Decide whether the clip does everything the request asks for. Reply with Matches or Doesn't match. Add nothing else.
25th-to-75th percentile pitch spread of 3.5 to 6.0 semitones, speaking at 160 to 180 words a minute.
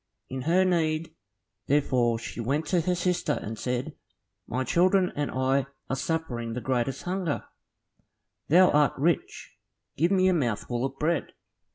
Doesn't match